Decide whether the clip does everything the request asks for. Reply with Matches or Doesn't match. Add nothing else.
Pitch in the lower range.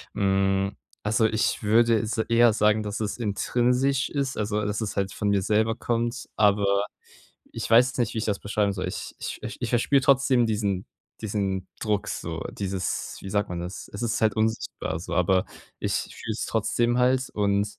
Matches